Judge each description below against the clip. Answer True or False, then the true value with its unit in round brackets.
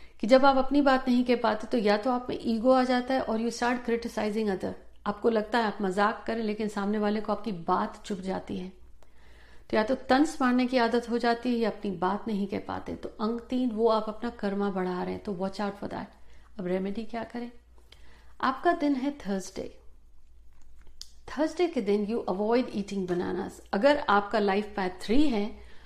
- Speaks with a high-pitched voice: True (220 Hz)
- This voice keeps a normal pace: False (210 wpm)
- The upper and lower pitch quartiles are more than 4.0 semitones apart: False (3.6 semitones)